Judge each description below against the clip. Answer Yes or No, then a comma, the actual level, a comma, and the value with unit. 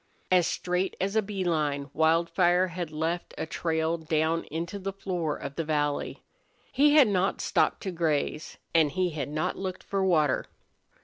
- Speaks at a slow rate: No, average, 170 wpm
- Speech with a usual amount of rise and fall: Yes, average, 3.0 semitones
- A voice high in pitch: No, medium, 170 Hz